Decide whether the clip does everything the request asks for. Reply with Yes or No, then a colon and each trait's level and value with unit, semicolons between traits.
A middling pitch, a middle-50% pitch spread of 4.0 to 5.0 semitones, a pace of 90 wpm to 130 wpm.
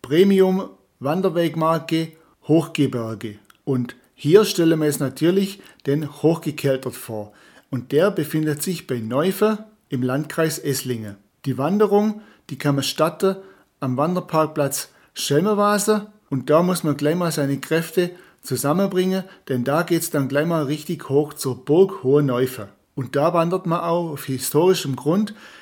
No: medium, 155 Hz; average, 4.7 semitones; average, 140 wpm